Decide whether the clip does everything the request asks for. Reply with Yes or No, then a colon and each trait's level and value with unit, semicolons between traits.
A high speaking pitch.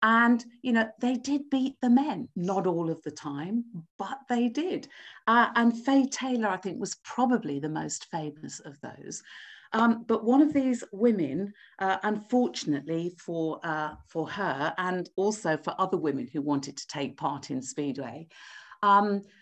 Yes: high, 205 Hz